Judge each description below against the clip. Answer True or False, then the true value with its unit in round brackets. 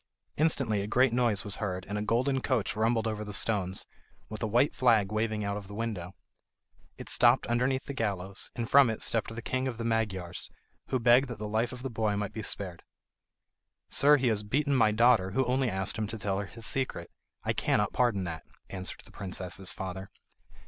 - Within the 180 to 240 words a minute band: True (205 wpm)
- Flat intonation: False (3.3 semitones)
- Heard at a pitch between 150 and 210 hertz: False (110 Hz)